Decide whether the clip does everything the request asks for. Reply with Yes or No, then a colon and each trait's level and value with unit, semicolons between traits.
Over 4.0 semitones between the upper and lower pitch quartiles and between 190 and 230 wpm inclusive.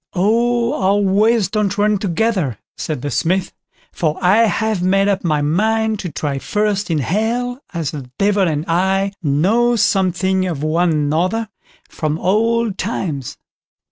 No: average, 4.7 semitones; average, 145 wpm